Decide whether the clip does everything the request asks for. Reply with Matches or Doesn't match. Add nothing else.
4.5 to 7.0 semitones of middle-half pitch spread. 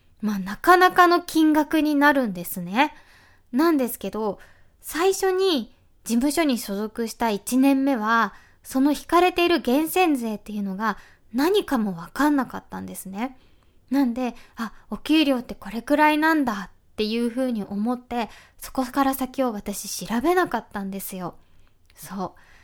Matches